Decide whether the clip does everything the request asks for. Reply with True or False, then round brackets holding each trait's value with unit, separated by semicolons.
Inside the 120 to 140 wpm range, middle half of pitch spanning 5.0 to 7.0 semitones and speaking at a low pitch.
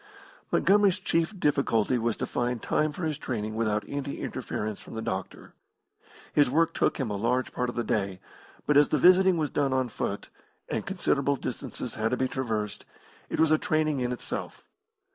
False (185 wpm; 5.5 semitones; 130 Hz)